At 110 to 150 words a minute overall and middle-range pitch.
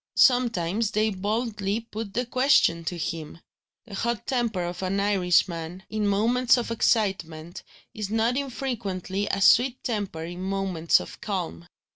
No: average, 140 wpm; high, 200 Hz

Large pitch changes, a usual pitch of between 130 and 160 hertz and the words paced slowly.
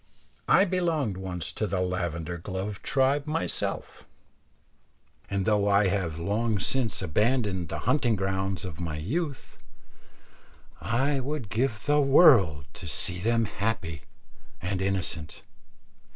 No: wide, 6.0 semitones; low, 100 Hz; slow, 125 wpm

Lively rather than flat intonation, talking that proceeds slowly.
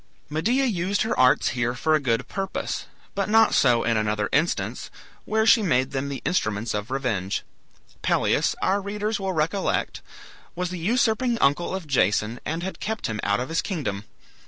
No: wide, 8.6 semitones; average, 175 wpm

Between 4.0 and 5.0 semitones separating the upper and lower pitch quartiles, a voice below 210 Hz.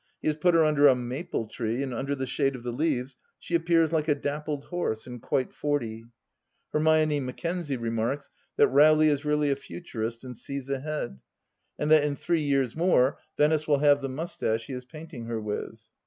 No: average, 3.5 semitones; medium, 140 Hz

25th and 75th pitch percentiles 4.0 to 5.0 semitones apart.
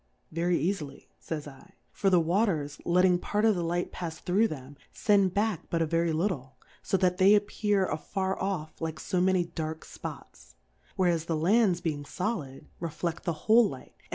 No: average, 3.5 semitones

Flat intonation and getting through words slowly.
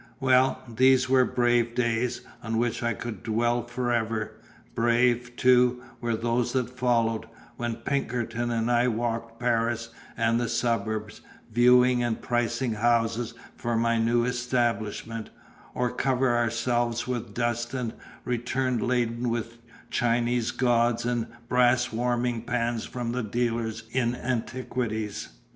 Yes: narrow, 1.2 semitones; slow, 125 wpm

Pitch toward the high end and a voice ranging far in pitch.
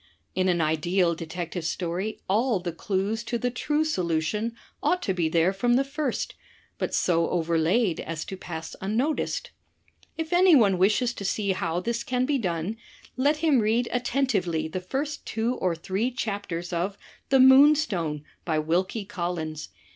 Yes: high, 195 Hz; wide, 6.4 semitones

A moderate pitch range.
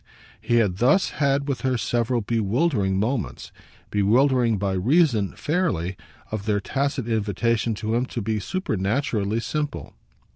Yes: average, 4.6 semitones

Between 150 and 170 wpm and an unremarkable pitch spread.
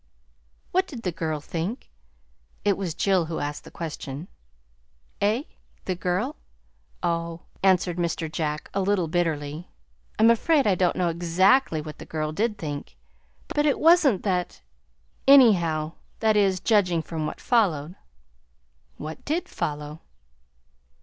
No: slow, 135 wpm; average, 4.7 semitones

